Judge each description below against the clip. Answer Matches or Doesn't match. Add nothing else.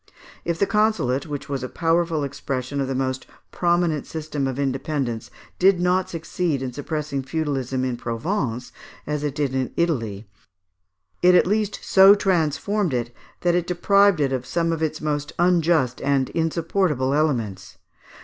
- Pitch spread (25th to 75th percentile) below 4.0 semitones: Doesn't match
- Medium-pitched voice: Matches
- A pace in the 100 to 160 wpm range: Matches